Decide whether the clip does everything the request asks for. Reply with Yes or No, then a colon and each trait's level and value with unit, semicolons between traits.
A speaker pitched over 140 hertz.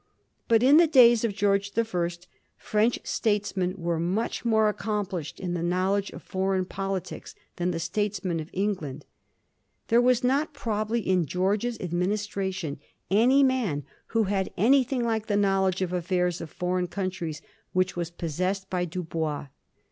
Yes: high, 190 Hz